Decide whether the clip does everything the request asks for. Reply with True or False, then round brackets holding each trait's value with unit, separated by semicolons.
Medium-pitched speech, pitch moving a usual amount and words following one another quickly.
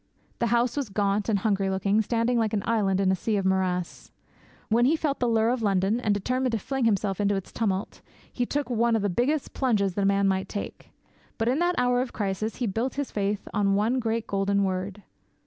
False (215 Hz; 3.5 semitones; 225 wpm)